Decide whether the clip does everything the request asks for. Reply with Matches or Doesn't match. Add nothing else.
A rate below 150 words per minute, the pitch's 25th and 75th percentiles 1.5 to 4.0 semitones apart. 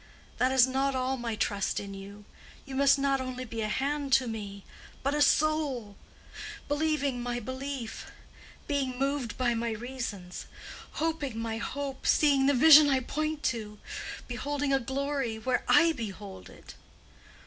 Matches